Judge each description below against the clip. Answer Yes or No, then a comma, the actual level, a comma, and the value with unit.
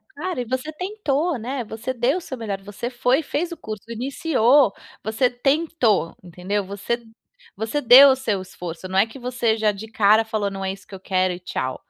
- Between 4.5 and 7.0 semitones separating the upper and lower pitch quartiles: Yes, average, 5.0 semitones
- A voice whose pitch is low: No, high, 230 Hz